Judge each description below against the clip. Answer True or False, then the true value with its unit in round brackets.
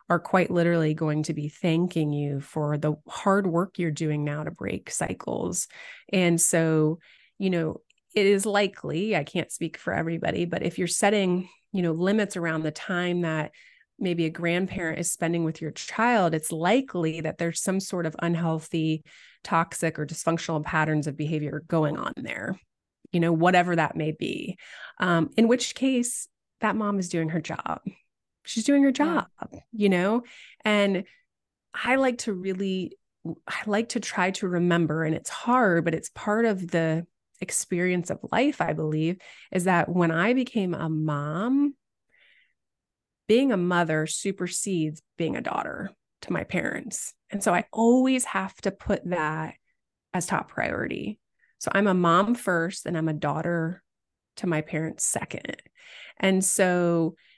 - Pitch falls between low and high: True (175 Hz)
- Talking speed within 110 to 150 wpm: False (160 wpm)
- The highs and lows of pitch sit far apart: False (4.0 semitones)